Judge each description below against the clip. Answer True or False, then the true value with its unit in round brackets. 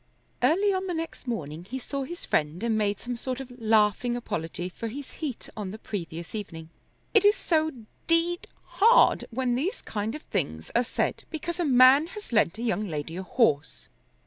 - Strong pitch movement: True (7.8 semitones)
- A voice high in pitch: True (240 Hz)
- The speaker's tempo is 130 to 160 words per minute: False (190 wpm)